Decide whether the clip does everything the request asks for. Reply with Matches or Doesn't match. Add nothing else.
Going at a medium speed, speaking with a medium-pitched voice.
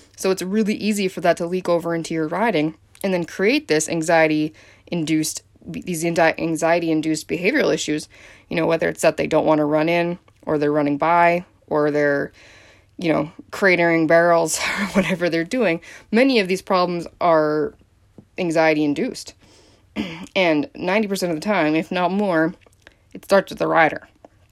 Matches